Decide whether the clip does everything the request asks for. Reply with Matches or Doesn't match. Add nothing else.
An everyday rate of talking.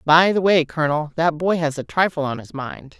Doesn't match